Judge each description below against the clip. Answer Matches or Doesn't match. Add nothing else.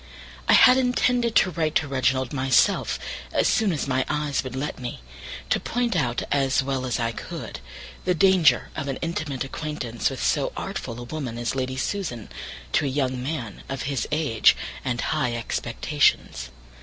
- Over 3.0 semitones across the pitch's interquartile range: Matches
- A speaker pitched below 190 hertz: Matches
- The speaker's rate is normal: Matches